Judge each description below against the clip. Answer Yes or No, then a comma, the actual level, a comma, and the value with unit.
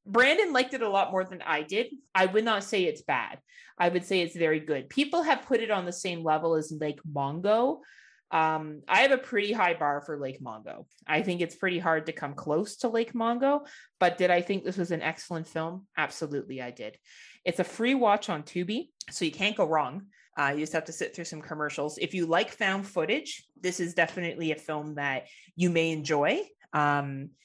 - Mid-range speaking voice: Yes, medium, 175 Hz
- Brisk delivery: Yes, fast, 220 wpm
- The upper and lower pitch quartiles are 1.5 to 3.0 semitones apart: No, average, 5.3 semitones